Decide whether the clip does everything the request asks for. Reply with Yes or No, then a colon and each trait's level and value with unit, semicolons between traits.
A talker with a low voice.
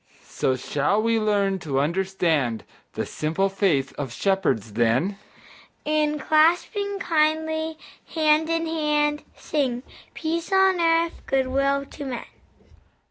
No: very high, 270 Hz